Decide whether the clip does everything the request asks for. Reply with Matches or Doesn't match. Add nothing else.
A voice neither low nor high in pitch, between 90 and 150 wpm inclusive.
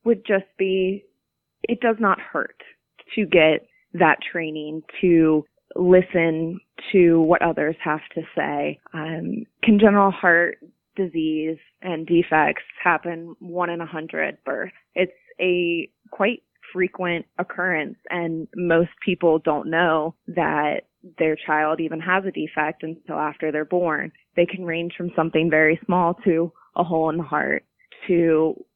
Matches